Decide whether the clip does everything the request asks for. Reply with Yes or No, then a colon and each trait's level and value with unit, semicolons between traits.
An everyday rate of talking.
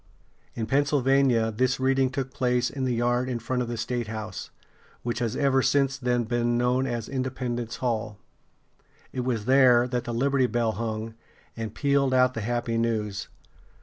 Yes: average, 165 wpm